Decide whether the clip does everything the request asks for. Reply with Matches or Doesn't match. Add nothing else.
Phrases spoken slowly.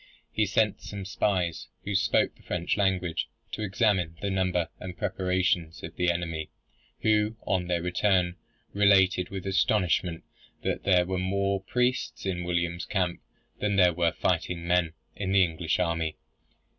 Doesn't match